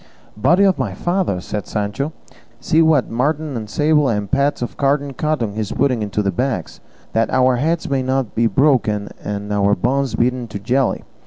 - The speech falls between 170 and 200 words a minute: Yes, average, 185 wpm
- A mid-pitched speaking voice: No, low, 125 Hz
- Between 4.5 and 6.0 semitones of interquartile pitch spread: Yes, average, 5.2 semitones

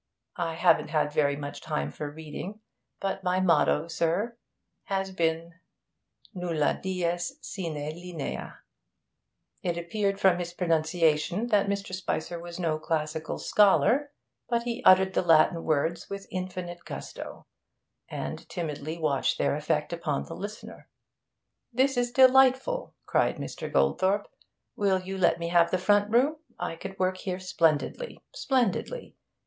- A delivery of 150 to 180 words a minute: No, slow, 135 wpm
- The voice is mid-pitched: Yes, medium, 180 Hz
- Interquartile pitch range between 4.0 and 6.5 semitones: No, average, 3.6 semitones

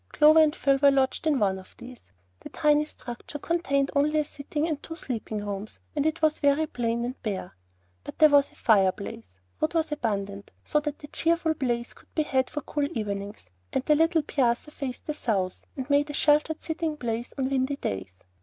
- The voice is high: Yes, very high, 275 Hz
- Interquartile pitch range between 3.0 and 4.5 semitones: No, average, 5.0 semitones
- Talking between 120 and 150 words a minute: No, average, 200 wpm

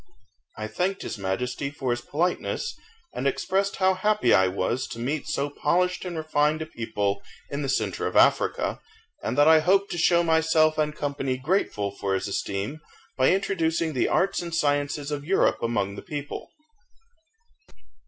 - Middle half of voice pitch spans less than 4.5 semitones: No, wide, 5.5 semitones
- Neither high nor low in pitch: Yes, medium, 150 Hz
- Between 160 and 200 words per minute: Yes, average, 165 wpm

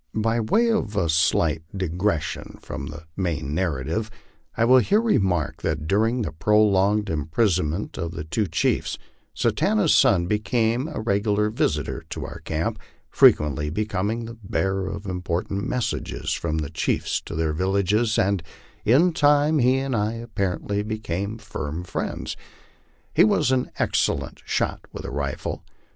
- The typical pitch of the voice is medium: No, low, 100 Hz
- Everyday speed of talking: Yes, average, 145 wpm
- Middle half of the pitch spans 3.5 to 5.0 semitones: No, wide, 5.4 semitones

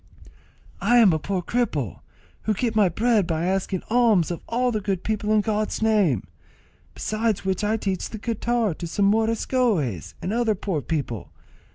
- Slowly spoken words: No, average, 165 wpm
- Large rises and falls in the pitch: No, average, 4.1 semitones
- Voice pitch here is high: Yes, high, 210 Hz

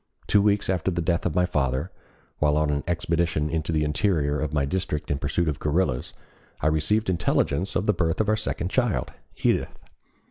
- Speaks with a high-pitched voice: No, very low, 85 Hz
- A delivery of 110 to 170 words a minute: No, average, 190 wpm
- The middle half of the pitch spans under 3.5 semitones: No, average, 4.0 semitones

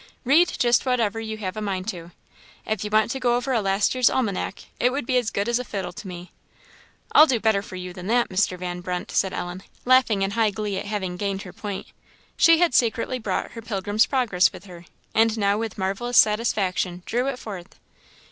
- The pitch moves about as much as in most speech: Yes, average, 4.0 semitones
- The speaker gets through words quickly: Yes, fast, 215 wpm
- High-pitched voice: Yes, high, 210 Hz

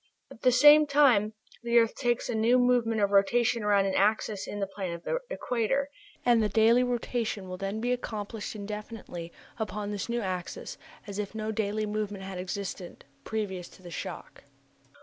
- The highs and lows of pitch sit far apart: No, average, 3.2 semitones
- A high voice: Yes, high, 215 Hz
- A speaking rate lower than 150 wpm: No, average, 180 wpm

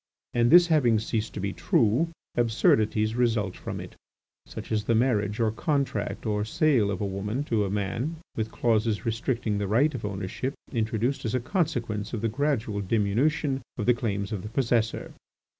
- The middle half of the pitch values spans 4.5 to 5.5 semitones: No, average, 3.3 semitones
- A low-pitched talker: Yes, low, 115 Hz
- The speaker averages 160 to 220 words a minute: Yes, average, 175 wpm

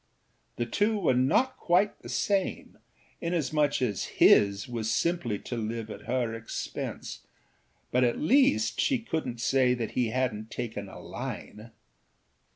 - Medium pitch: No, low, 125 Hz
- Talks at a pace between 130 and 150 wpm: Yes, average, 140 wpm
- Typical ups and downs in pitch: No, wide, 6.8 semitones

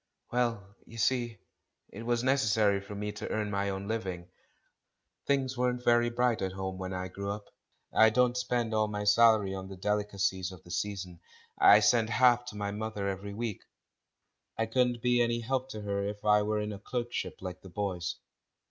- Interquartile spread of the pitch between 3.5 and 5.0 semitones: No, average, 3.1 semitones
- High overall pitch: No, low, 105 Hz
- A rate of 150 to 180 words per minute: No, average, 190 wpm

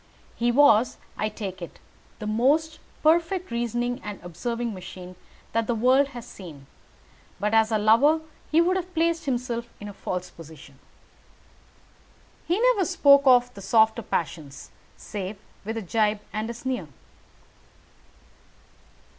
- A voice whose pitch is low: No, high, 230 Hz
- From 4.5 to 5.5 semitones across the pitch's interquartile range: Yes, average, 5.1 semitones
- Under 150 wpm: Yes, average, 140 wpm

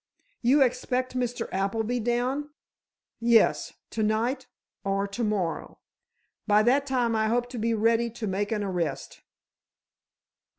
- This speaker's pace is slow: Yes, slow, 130 wpm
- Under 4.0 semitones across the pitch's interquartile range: Yes, average, 2.8 semitones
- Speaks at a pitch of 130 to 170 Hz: No, high, 230 Hz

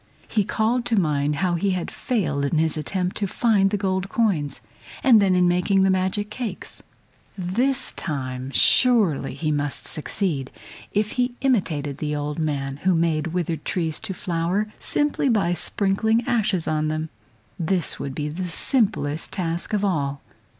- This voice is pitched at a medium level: Yes, medium, 180 Hz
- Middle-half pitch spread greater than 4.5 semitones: Yes, average, 5.2 semitones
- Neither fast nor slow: Yes, average, 160 wpm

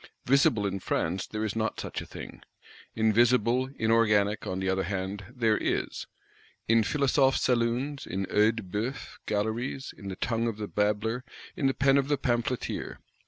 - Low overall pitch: Yes, low, 115 Hz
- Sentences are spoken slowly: No, average, 165 wpm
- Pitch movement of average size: Yes, average, 3.6 semitones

